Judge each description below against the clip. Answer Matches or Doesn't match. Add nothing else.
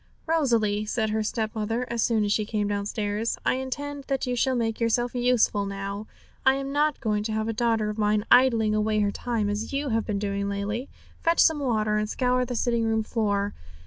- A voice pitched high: Matches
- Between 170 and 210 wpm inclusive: Matches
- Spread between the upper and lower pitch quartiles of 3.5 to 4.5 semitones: Doesn't match